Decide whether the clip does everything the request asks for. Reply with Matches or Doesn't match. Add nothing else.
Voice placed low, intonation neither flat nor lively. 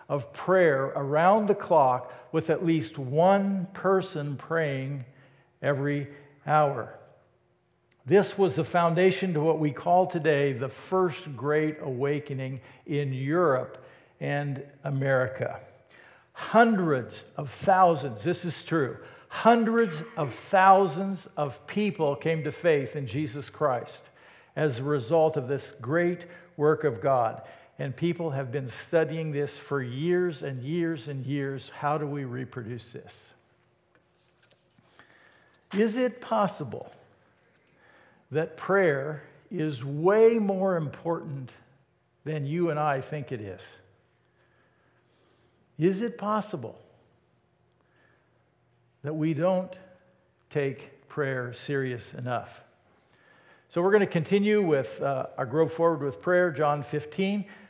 Doesn't match